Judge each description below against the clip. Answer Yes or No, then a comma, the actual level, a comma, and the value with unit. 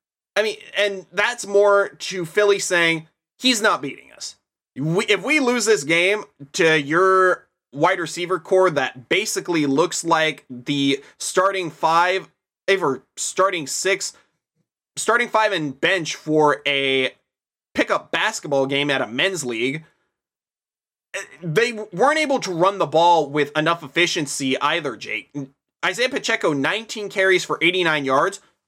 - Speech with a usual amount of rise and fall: Yes, average, 4.7 semitones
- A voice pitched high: No, medium, 180 Hz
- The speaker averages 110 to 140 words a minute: Yes, slow, 135 wpm